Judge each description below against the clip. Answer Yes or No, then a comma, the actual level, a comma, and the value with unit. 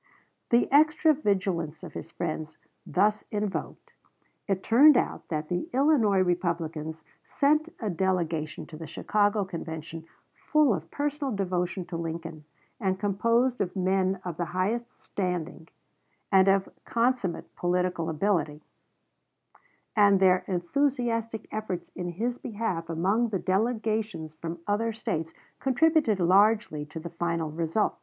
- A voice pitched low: No, high, 190 Hz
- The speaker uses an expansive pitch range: No, average, 5.0 semitones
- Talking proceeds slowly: Yes, slow, 130 wpm